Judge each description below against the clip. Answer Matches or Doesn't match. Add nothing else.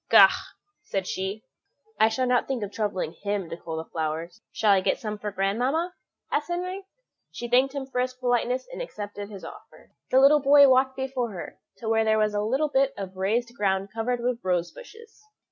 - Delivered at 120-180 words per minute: Doesn't match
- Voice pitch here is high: Matches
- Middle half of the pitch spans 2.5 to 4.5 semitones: Doesn't match